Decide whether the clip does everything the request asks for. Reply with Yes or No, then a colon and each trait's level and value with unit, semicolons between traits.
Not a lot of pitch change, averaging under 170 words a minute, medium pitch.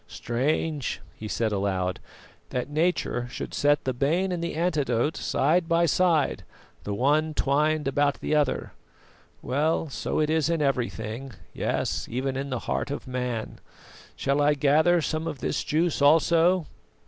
No: average, 3.8 semitones; average, 150 wpm; medium, 145 Hz